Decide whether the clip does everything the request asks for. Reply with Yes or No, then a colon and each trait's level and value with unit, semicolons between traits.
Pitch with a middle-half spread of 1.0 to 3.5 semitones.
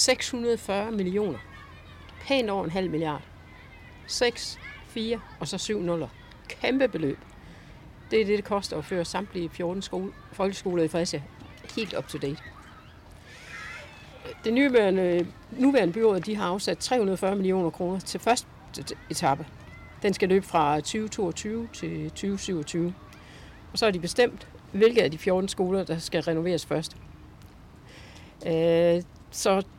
No: average, 4.6 semitones